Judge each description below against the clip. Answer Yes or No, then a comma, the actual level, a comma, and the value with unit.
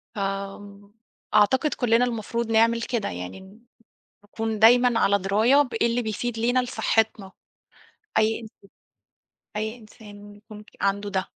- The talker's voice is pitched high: Yes, high, 220 Hz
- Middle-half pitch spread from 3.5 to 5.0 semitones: No, narrow, 2.4 semitones